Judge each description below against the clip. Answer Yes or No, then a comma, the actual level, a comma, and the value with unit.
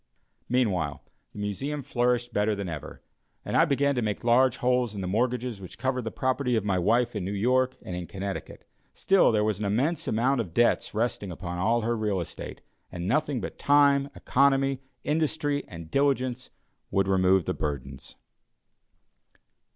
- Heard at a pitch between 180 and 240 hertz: No, low, 115 Hz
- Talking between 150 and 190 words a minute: Yes, average, 170 wpm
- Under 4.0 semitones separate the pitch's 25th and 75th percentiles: No, average, 5.0 semitones